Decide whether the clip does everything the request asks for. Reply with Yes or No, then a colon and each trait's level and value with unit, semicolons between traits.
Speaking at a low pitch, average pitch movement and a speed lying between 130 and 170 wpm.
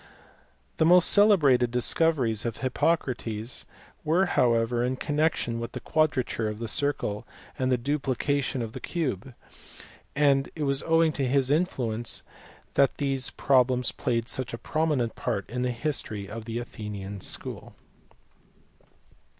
Yes: low, 130 Hz; average, 4.0 semitones; average, 140 wpm